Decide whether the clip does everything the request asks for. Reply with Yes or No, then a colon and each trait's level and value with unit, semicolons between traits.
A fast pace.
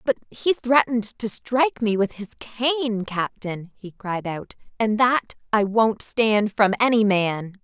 No: average, 165 wpm